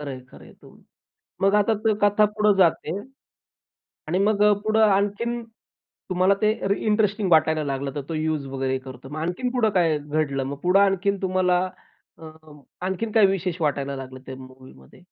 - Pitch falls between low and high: Yes, medium, 175 Hz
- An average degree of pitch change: No, wide, 6.0 semitones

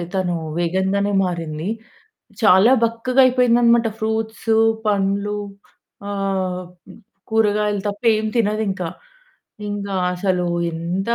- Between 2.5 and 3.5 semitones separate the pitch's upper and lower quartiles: Yes, average, 2.8 semitones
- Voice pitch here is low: No, high, 200 Hz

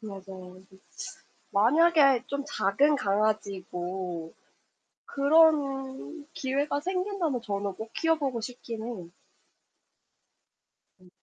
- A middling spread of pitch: No, wide, 6.7 semitones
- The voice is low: No, high, 240 Hz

